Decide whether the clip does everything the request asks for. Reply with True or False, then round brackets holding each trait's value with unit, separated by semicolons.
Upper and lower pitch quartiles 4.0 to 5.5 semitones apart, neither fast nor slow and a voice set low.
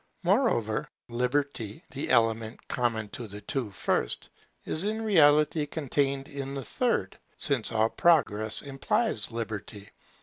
False (5.0 semitones; 125 wpm; 130 Hz)